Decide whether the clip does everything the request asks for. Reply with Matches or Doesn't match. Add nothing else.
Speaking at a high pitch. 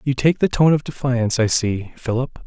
Doesn't match